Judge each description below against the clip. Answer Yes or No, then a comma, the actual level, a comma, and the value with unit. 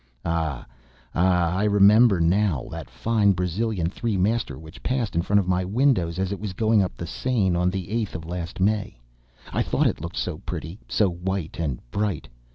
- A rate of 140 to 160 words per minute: No, average, 190 wpm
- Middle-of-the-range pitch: No, very low, 95 Hz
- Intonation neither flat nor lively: Yes, average, 3.7 semitones